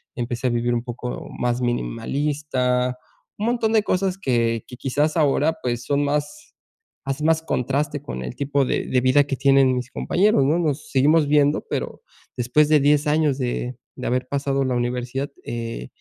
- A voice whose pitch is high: No, low, 135 Hz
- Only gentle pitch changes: No, average, 3.2 semitones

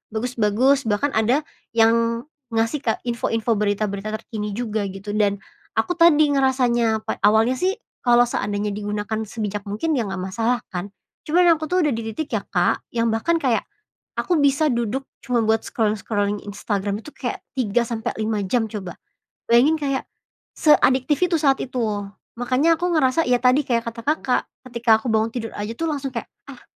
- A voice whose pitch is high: Yes, high, 230 Hz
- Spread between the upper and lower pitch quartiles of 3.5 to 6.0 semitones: Yes, average, 3.9 semitones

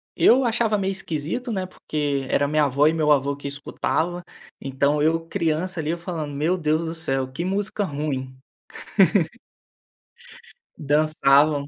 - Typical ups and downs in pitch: Yes, average, 3.6 semitones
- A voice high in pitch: No, medium, 155 Hz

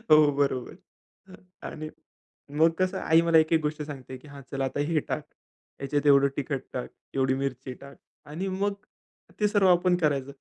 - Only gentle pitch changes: No, average, 3.4 semitones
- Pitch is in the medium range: Yes, medium, 150 Hz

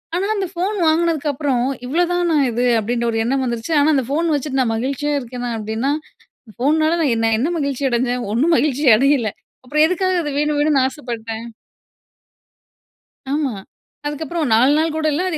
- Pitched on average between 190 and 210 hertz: No, very high, 280 Hz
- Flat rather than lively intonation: No, average, 4.3 semitones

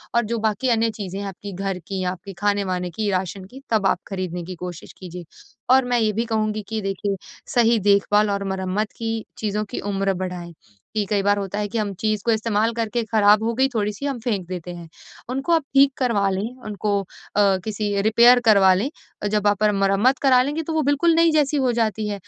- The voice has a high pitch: Yes, high, 210 Hz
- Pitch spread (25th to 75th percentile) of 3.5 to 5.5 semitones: No, average, 3.0 semitones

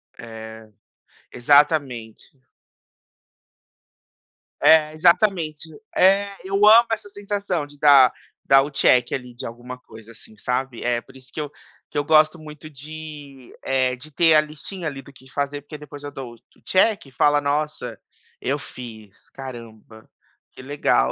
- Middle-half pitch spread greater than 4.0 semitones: No, average, 3.7 semitones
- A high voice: No, medium, 145 Hz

